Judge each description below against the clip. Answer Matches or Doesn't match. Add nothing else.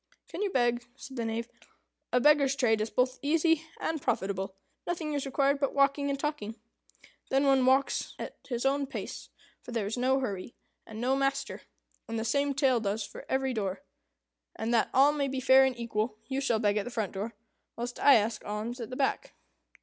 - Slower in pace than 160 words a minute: Doesn't match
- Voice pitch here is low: Doesn't match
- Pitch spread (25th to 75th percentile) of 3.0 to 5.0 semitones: Matches